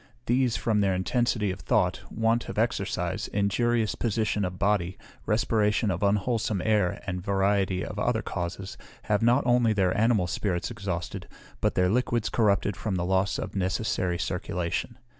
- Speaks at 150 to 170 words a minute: Yes, average, 160 wpm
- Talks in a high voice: No, low, 100 Hz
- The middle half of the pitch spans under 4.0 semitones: Yes, average, 3.4 semitones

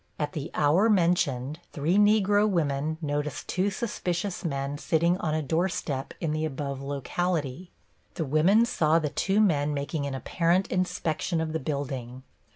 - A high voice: No, medium, 155 Hz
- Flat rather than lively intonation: No, average, 4.1 semitones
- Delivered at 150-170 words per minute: Yes, average, 160 wpm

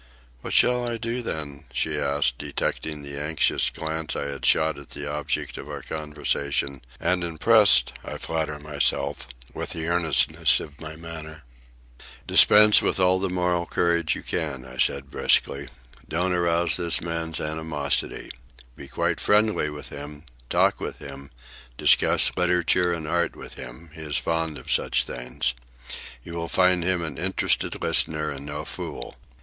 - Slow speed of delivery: No, average, 155 wpm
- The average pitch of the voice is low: Yes, very low, 80 Hz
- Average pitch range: Yes, average, 3.1 semitones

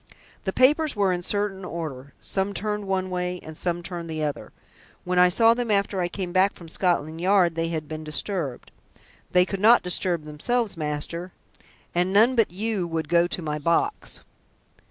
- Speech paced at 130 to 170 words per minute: No, average, 180 wpm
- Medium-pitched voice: Yes, medium, 180 Hz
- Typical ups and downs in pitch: Yes, average, 3.4 semitones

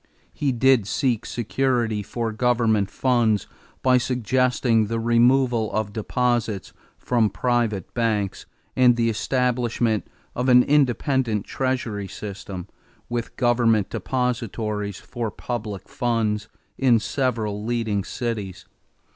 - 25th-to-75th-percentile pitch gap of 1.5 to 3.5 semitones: Yes, average, 2.7 semitones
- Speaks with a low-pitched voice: Yes, low, 115 Hz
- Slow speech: Yes, slow, 105 wpm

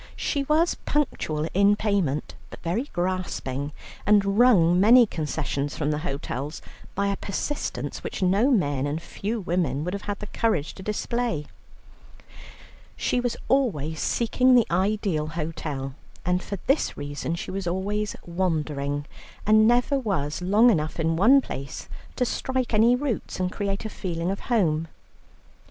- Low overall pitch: No, high, 190 Hz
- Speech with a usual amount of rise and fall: No, wide, 6.1 semitones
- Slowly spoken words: No, average, 150 wpm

